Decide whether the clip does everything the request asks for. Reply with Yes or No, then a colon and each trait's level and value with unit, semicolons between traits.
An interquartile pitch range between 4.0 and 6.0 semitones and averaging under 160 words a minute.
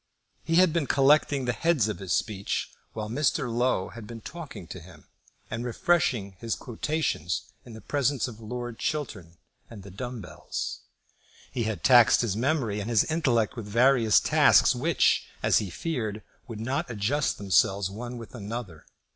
No: average, 4.5 semitones; average, 165 wpm